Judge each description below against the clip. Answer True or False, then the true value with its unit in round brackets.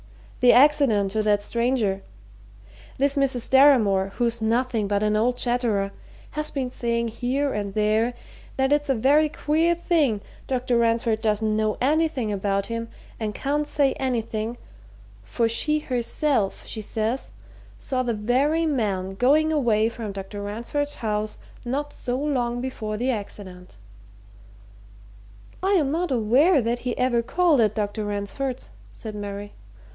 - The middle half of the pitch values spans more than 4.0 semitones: True (4.4 semitones)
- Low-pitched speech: False (235 Hz)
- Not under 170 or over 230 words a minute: False (140 wpm)